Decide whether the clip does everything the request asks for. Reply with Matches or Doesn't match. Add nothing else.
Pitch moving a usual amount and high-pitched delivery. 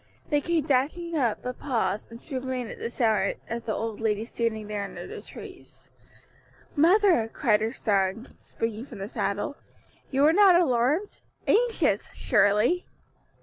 Doesn't match